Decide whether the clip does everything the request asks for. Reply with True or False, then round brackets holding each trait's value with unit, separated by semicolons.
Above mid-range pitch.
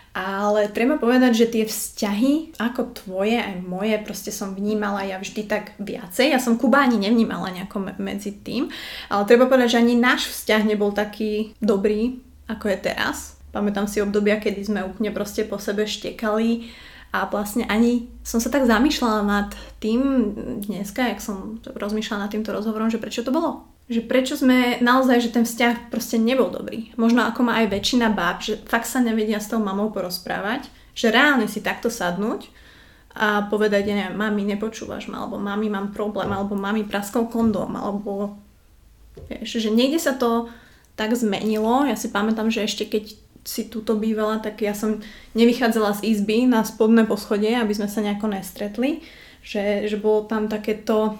True (220 Hz)